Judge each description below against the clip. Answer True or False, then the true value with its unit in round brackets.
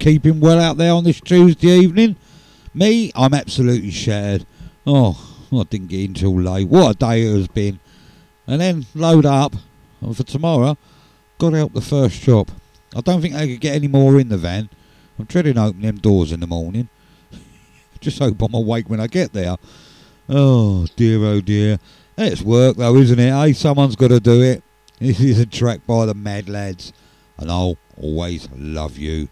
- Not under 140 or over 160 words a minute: False (190 wpm)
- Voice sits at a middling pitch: False (120 Hz)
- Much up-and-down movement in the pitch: True (6.1 semitones)